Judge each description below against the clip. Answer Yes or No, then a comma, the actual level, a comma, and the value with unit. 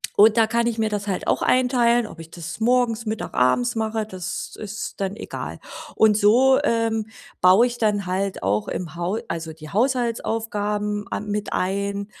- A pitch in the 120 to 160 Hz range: No, high, 210 Hz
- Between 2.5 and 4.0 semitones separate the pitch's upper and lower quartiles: Yes, average, 2.9 semitones